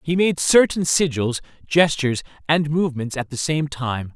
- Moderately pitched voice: Yes, medium, 145 Hz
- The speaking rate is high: No, average, 160 wpm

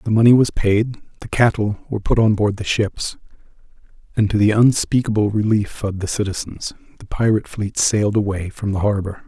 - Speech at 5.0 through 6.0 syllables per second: Yes, 5.5 syllables/s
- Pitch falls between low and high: No, low, 105 Hz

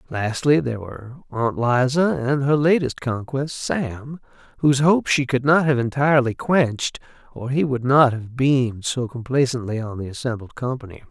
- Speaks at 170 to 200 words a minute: No, average, 160 wpm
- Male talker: Yes, male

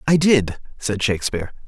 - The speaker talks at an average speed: Yes, average, 145 wpm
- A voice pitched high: No, low, 120 Hz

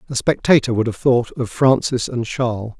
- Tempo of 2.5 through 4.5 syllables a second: No, 5.0 syllables/s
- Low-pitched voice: Yes, low, 125 Hz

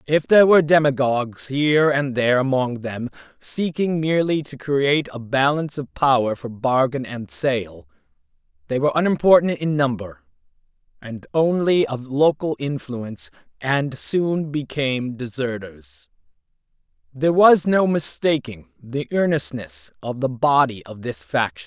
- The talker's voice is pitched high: No, medium, 140 Hz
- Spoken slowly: Yes, slow, 130 wpm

